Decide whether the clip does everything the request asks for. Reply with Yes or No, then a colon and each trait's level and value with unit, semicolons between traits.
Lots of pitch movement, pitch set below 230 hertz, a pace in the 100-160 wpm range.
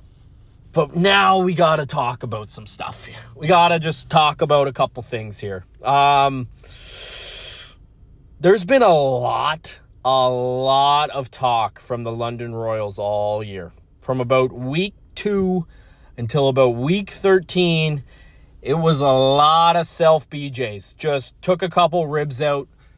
Yes: wide, 5.7 semitones; medium, 140 Hz; average, 145 wpm